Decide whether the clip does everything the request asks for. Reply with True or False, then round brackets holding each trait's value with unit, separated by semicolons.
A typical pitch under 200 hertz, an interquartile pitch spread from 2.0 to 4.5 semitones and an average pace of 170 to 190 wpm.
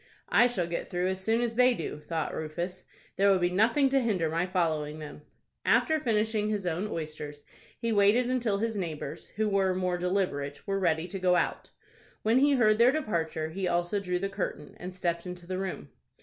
False (185 Hz; 4.2 semitones; 200 wpm)